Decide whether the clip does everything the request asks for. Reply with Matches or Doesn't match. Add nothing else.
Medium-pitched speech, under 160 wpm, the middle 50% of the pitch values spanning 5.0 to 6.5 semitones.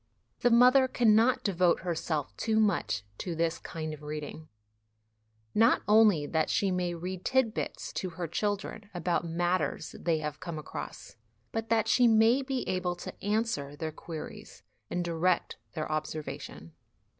Matches